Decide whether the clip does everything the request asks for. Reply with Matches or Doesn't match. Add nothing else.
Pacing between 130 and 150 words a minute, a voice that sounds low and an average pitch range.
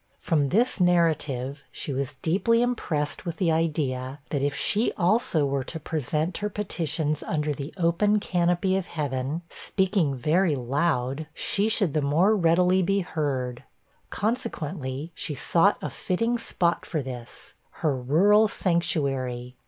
Doesn't match